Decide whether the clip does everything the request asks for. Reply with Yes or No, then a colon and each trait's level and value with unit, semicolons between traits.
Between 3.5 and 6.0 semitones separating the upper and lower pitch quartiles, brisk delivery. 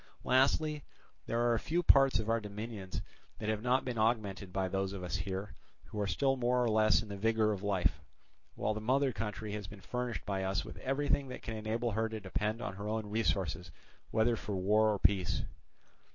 No: average, 3.1 semitones; fast, 210 wpm